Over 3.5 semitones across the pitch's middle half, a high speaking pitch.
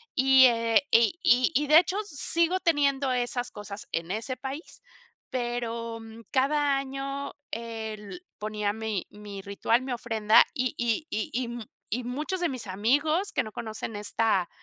Yes: average, 4.0 semitones; high, 240 Hz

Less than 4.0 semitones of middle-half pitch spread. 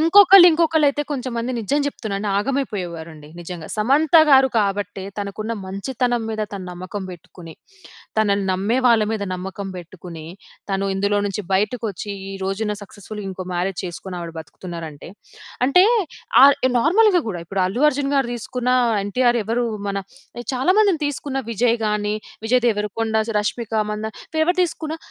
No: average, 5.3 semitones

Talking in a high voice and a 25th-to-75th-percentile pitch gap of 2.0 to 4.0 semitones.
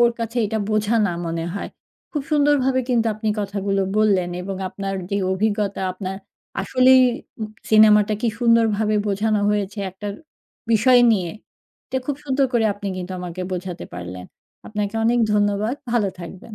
Yes: high, 210 Hz; average, 2.9 semitones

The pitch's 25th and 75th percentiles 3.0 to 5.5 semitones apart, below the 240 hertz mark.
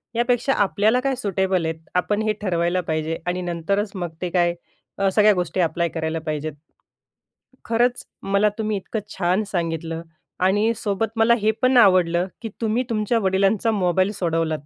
Yes: average, 4.0 semitones; high, 190 Hz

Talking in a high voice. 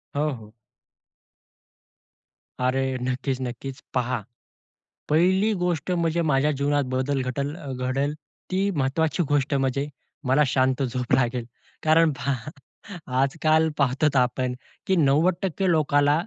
No: medium, 140 Hz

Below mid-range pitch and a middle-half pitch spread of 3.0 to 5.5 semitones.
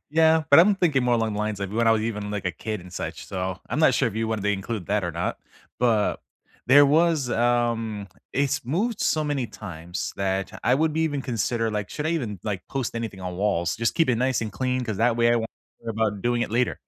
Yes: low, 115 Hz; average, 4.3 semitones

